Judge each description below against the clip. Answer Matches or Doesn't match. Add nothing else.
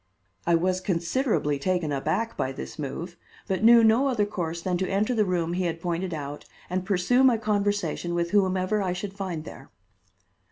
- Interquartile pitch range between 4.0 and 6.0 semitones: Doesn't match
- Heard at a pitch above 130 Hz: Matches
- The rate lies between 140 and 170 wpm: Doesn't match